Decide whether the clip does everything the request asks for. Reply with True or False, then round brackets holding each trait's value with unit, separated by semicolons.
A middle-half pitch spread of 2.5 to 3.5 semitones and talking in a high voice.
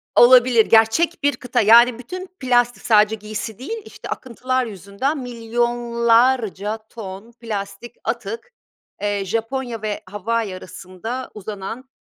True (2.8 semitones; 230 Hz)